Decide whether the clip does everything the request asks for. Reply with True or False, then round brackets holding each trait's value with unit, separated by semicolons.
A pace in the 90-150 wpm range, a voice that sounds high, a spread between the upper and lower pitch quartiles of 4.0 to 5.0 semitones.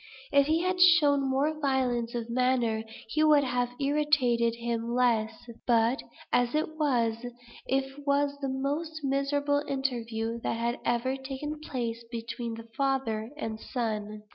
False (140 wpm; 260 Hz; 3.5 semitones)